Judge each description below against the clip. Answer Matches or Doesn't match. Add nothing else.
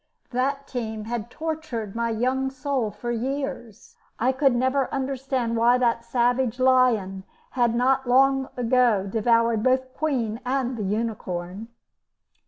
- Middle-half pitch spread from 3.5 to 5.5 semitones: Doesn't match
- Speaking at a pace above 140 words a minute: Doesn't match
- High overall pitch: Matches